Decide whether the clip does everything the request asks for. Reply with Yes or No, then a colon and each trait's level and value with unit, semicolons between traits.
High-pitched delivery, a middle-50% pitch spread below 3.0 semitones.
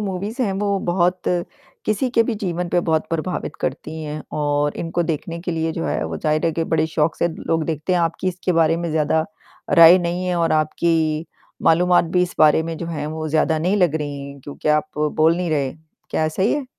No: medium, 165 Hz; narrow, 2.5 semitones